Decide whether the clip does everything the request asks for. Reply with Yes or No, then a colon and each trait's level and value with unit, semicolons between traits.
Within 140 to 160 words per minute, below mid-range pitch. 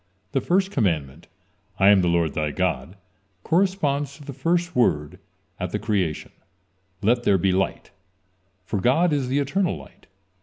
Yes: average, 155 wpm; low, 120 Hz